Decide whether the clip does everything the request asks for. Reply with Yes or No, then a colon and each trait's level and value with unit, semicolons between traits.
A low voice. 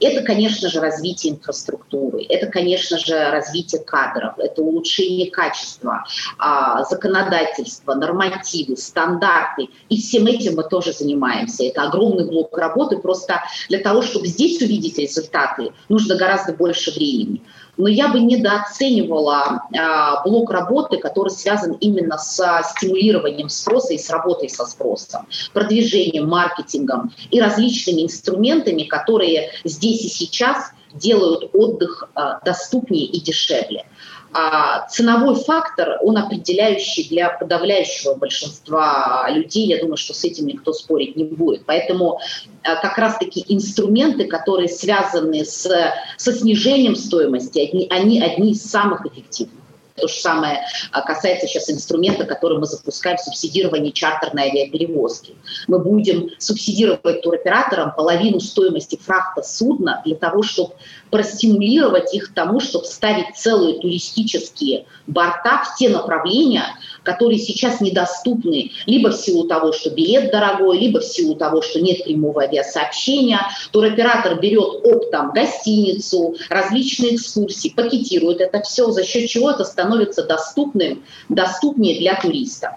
No: high, 190 Hz